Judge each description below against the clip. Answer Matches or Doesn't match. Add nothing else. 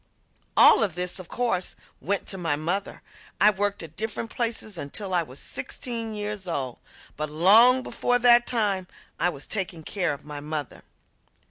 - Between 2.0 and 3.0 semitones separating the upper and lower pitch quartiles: Doesn't match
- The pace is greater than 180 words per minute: Doesn't match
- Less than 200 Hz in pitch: Matches